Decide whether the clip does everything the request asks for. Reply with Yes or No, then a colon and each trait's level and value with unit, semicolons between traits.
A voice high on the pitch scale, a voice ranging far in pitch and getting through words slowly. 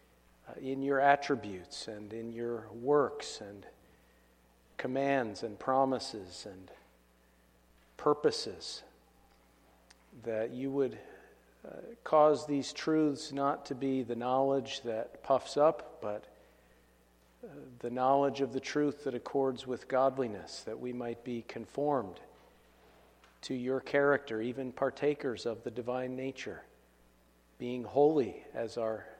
No: low, 125 Hz; wide, 6.1 semitones; slow, 115 wpm